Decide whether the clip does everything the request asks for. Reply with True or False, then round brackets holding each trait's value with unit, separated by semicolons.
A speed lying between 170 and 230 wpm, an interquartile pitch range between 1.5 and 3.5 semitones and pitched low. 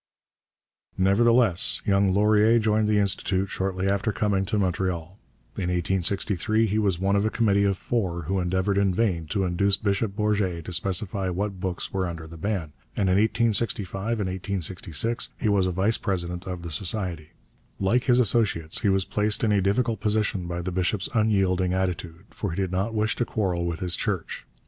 True (180 wpm; 2.6 semitones; 95 Hz)